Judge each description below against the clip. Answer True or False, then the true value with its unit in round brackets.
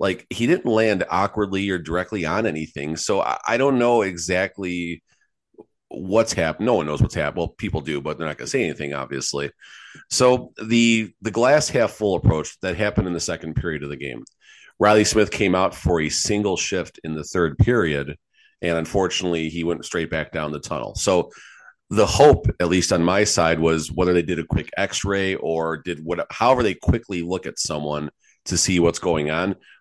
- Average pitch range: True (3.9 semitones)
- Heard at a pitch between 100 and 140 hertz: False (90 Hz)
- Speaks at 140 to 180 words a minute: False (195 wpm)